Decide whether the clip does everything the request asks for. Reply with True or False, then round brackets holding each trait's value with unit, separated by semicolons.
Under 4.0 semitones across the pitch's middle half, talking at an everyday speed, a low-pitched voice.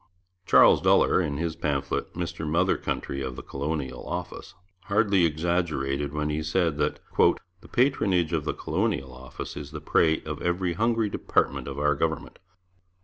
True (3.3 semitones; 155 wpm; 80 Hz)